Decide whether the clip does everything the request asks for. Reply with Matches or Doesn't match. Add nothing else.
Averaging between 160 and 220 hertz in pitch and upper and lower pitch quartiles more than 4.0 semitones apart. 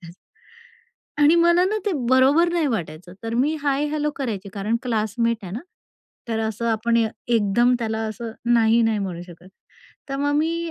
Doesn't match